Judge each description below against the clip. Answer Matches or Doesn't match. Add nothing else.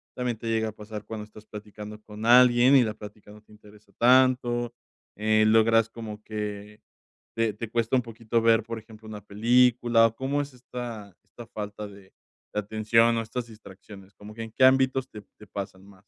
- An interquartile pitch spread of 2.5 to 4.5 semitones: Doesn't match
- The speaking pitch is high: Doesn't match